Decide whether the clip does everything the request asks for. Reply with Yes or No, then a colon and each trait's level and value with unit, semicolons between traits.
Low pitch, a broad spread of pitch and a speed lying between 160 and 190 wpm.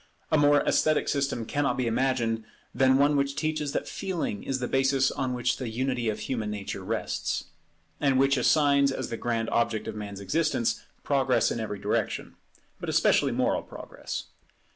No: low, 130 Hz; average, 3.5 semitones; average, 170 wpm